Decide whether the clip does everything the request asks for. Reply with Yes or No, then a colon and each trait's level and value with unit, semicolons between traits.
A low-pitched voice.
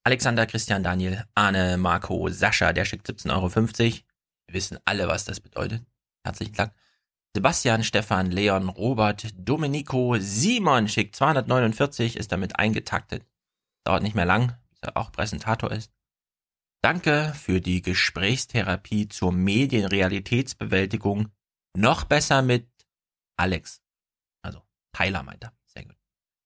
Yes: low, 110 Hz